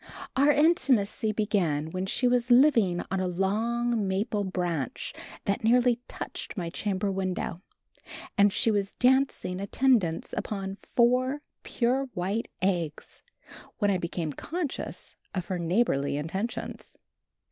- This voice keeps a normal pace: No, slow, 125 wpm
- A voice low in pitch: No, high, 200 Hz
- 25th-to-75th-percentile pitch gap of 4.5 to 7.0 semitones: Yes, average, 4.8 semitones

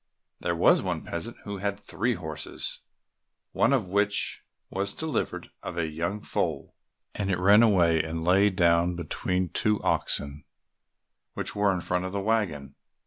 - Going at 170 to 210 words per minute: No, average, 155 wpm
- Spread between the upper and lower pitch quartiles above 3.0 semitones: Yes, average, 3.4 semitones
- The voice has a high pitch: No, very low, 95 Hz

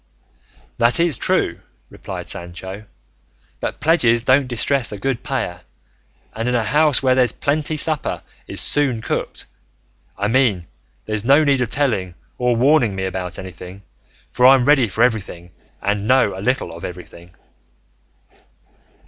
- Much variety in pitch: Yes, wide, 5.7 semitones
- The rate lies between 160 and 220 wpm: No, average, 145 wpm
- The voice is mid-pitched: No, low, 120 Hz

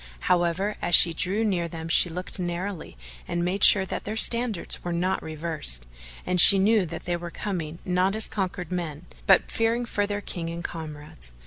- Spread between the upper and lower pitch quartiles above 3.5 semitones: No, average, 3.1 semitones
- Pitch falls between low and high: Yes, medium, 175 Hz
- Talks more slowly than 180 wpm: No, average, 190 wpm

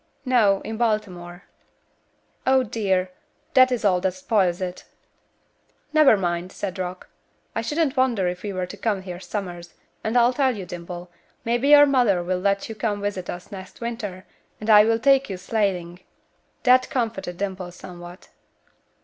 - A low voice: No, high, 200 Hz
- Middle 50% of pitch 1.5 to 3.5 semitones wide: No, average, 4.3 semitones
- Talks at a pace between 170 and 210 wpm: No, average, 160 wpm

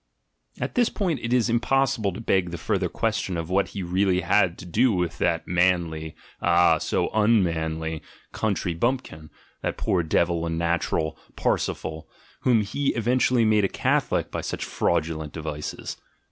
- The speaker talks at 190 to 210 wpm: No, average, 160 wpm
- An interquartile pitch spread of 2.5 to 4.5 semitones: No, average, 5.2 semitones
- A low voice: Yes, very low, 90 Hz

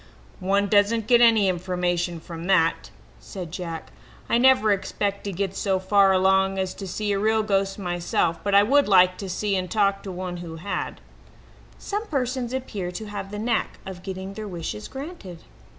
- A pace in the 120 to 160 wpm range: No, average, 180 wpm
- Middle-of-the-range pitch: No, high, 195 Hz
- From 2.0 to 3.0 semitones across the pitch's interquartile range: Yes, narrow, 2.6 semitones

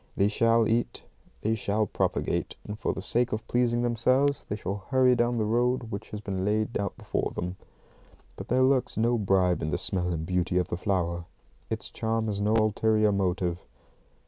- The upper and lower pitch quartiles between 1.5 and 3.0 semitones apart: No, average, 3.8 semitones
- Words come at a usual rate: Yes, average, 190 wpm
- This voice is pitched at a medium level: No, low, 105 Hz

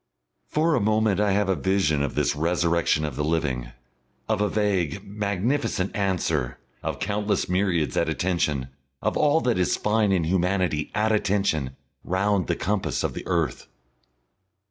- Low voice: Yes, very low, 95 Hz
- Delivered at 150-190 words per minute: Yes, average, 155 wpm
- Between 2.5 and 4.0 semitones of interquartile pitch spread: No, average, 4.4 semitones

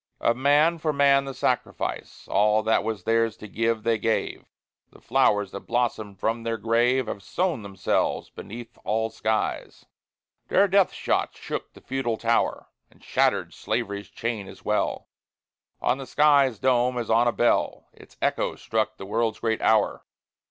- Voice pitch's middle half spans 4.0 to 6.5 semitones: No, average, 3.1 semitones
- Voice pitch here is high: No, low, 115 Hz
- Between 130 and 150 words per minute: No, average, 160 wpm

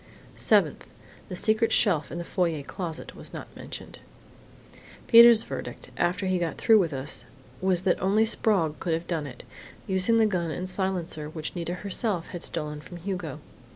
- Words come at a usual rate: Yes, average, 170 wpm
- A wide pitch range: No, average, 3.3 semitones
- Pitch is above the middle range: No, medium, 180 Hz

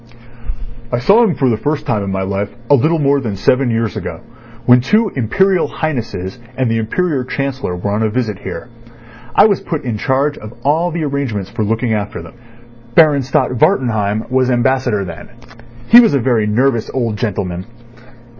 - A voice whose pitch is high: No, low, 125 Hz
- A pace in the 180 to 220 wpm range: Yes, average, 185 wpm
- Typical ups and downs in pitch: Yes, average, 4.9 semitones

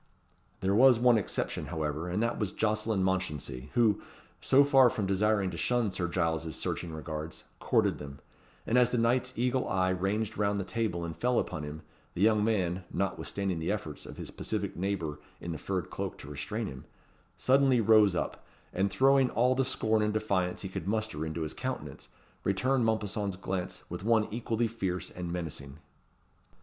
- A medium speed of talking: Yes, average, 180 wpm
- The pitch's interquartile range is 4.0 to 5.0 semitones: Yes, average, 4.6 semitones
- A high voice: No, low, 100 Hz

